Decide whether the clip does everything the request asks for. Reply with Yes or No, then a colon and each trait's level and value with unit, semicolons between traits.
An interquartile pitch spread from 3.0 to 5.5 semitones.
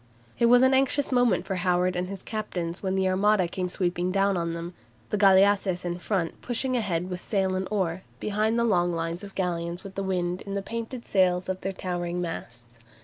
No: narrow, 2.6 semitones